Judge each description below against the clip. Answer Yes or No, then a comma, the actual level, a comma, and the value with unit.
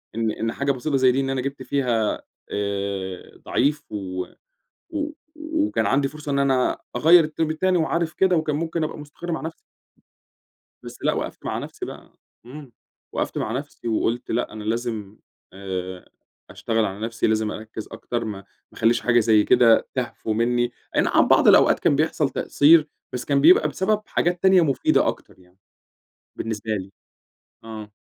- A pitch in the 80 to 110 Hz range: No, low, 125 Hz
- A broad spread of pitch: Yes, wide, 5.8 semitones